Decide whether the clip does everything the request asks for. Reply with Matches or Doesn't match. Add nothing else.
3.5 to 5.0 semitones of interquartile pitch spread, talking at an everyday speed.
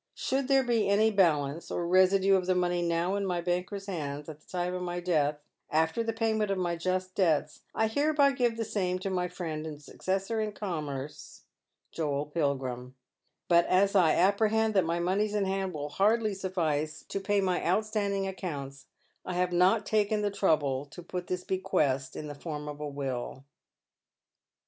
Matches